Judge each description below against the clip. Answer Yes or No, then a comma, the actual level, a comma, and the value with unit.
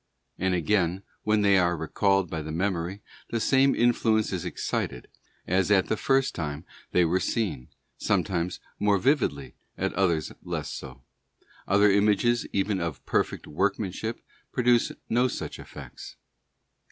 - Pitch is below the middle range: Yes, very low, 95 Hz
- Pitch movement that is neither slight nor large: Yes, average, 4.0 semitones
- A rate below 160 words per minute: Yes, average, 140 wpm